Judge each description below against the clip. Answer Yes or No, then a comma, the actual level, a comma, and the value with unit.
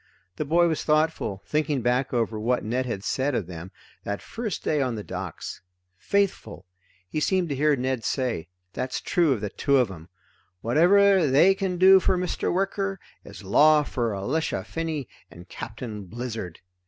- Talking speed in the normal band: Yes, average, 170 wpm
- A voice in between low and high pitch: No, low, 130 Hz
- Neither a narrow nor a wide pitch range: No, wide, 7.4 semitones